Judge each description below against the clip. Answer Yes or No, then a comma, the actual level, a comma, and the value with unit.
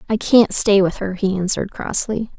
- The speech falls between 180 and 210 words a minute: Yes, average, 200 wpm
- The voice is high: Yes, high, 200 Hz